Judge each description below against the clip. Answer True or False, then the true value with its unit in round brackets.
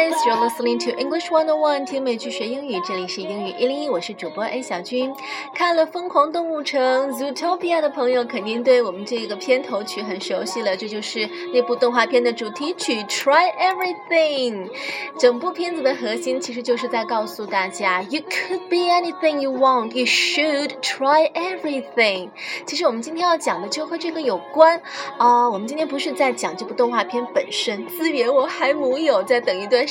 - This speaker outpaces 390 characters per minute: True (435 characters per minute)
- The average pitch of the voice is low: False (270 Hz)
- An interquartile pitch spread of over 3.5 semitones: True (4.9 semitones)